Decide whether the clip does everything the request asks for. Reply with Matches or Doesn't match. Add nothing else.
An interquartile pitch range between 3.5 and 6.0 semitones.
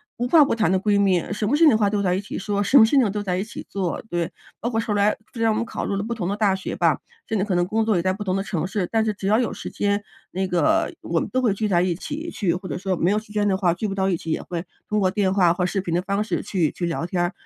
Doesn't match